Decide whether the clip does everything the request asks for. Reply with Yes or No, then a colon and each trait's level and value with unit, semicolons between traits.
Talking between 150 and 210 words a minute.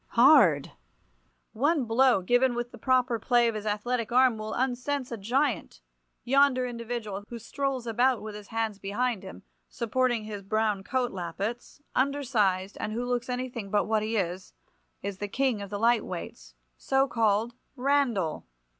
Yes: average, 155 wpm